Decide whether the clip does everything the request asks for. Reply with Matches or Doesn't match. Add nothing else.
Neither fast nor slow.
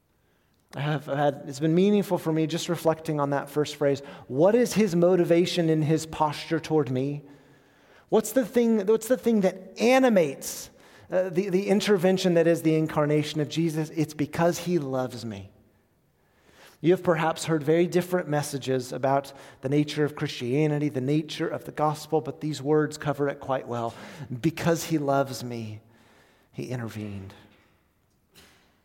Matches